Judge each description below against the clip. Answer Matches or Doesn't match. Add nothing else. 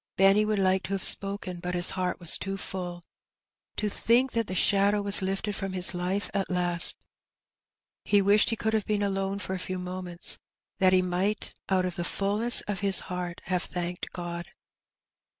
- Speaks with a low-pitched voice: Doesn't match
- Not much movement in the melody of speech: Matches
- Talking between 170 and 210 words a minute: Matches